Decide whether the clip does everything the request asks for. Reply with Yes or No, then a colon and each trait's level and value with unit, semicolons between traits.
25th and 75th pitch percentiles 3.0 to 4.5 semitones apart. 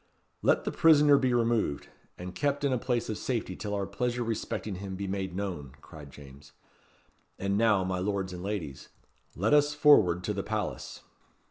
No: average, 5.0 semitones